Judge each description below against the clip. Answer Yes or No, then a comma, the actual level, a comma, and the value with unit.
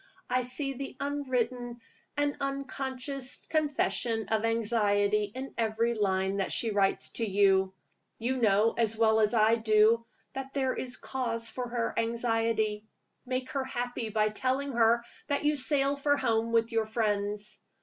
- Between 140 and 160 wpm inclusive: Yes, average, 150 wpm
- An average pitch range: Yes, average, 3.3 semitones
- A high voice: Yes, high, 230 Hz